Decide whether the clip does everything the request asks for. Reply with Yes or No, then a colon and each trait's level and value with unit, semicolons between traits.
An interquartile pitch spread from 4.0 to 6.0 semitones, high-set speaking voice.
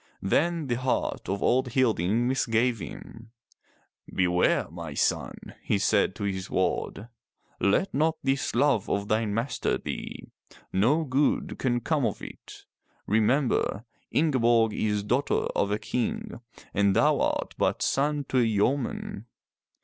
No: average, 4.7 semitones; low, 115 Hz